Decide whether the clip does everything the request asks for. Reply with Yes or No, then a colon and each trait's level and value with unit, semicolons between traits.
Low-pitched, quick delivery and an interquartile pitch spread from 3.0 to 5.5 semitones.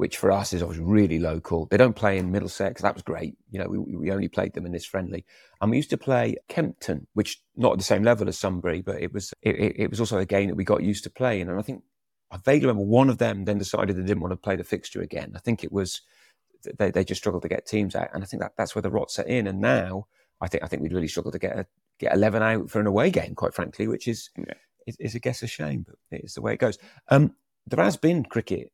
Yes: low, 100 Hz; fast, 280 wpm; average, 3.6 semitones